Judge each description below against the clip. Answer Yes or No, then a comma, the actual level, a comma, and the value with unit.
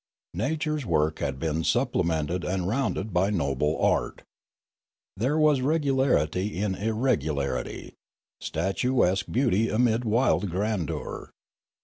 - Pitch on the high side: No, low, 100 Hz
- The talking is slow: Yes, slow, 110 wpm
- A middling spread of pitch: No, wide, 7.4 semitones